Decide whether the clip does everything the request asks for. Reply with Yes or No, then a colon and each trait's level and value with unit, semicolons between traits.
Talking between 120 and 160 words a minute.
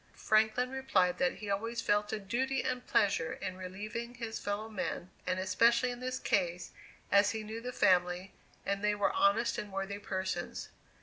No: average, 175 wpm